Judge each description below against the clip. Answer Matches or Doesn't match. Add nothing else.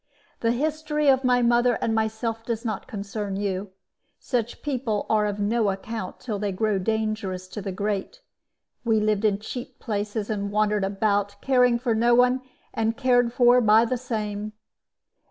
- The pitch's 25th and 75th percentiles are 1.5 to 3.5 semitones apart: Matches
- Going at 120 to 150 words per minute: Doesn't match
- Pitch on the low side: Doesn't match